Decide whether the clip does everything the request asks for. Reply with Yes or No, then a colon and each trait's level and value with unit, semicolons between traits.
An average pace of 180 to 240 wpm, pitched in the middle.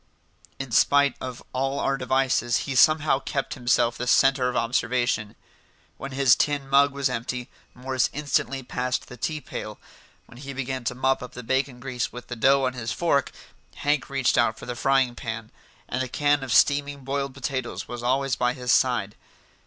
No: average, 185 wpm; low, 130 Hz